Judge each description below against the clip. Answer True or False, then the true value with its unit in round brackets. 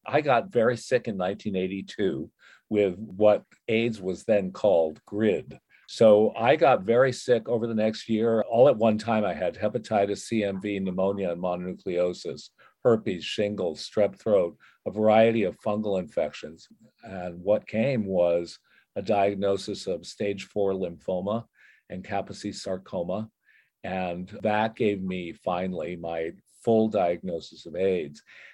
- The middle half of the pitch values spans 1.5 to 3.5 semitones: True (2.9 semitones)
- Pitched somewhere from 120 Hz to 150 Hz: False (100 Hz)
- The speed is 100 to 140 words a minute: True (135 wpm)